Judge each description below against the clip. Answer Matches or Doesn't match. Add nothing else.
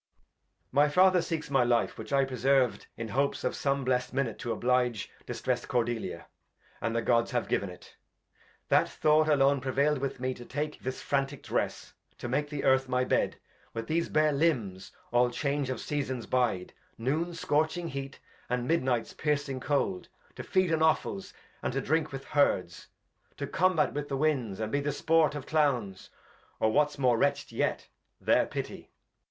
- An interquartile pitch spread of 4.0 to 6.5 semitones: Doesn't match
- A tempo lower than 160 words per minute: Doesn't match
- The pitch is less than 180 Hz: Matches